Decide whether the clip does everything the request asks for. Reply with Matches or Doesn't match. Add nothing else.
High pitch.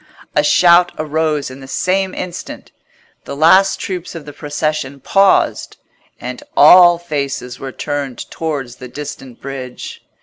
Doesn't match